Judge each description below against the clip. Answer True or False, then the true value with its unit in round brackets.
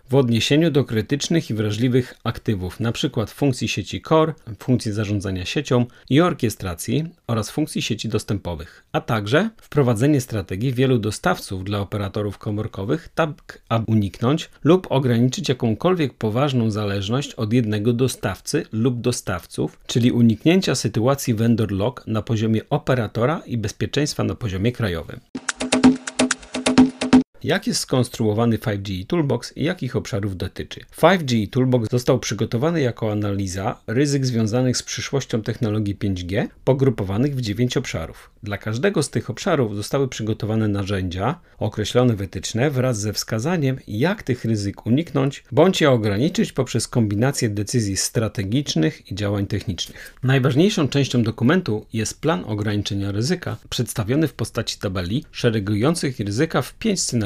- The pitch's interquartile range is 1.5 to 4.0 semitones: False (4.6 semitones)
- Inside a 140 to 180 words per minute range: False (130 wpm)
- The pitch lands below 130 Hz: True (120 Hz)